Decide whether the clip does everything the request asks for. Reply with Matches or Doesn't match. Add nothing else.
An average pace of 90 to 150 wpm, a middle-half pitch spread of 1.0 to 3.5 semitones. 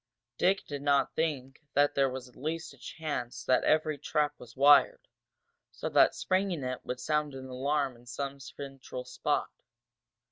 Doesn't match